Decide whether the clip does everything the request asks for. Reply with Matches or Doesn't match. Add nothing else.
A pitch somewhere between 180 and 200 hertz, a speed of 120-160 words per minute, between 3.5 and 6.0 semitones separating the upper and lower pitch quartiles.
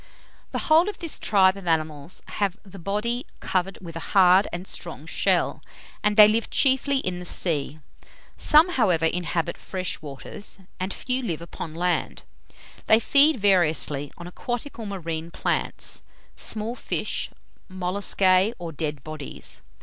Matches